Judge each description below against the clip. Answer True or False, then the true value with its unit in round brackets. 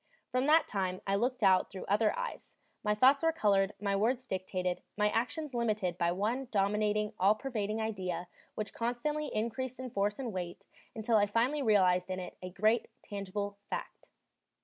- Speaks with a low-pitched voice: False (210 Hz)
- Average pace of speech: True (170 wpm)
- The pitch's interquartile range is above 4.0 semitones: False (3.6 semitones)